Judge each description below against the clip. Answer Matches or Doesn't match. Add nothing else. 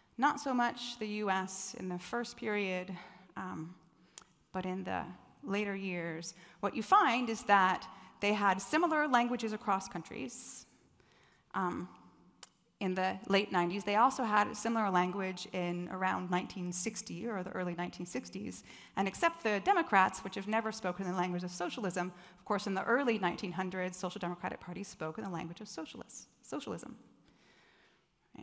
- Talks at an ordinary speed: Matches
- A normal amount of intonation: Matches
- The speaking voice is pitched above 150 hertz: Matches